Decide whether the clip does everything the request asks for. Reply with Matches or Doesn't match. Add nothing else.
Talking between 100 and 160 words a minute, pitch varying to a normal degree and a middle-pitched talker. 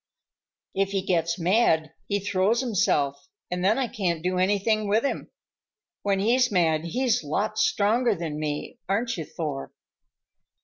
Doesn't match